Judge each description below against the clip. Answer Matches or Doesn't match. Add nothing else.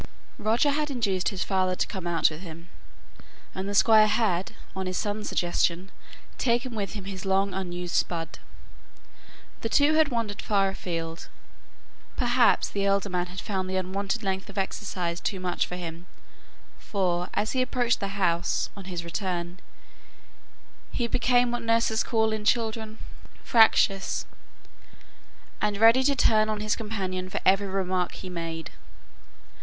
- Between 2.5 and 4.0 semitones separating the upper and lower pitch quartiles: Matches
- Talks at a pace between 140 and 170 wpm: Matches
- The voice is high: Matches